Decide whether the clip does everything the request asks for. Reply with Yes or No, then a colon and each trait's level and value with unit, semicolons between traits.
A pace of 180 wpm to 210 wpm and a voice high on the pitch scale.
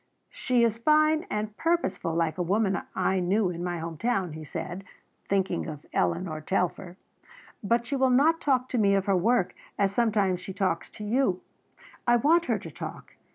Yes: average, 185 wpm; high, 200 Hz